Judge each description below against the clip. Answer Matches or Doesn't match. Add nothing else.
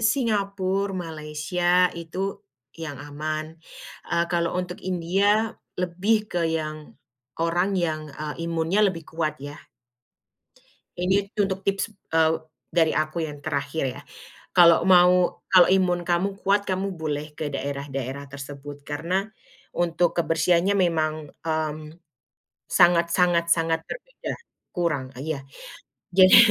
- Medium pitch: Matches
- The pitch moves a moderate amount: Matches